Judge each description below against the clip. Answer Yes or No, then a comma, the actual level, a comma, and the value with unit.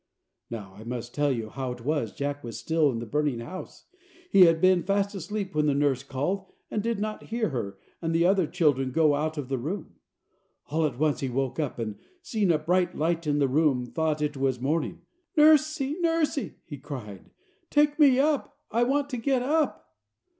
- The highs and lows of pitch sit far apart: Yes, wide, 7.0 semitones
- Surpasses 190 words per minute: Yes, average, 200 wpm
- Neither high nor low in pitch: Yes, medium, 155 Hz